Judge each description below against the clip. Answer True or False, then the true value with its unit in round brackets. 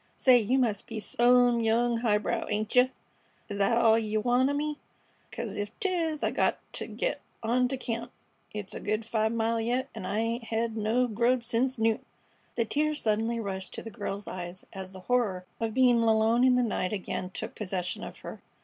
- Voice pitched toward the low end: False (230 Hz)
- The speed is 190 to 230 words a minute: True (200 wpm)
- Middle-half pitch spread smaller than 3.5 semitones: True (2.7 semitones)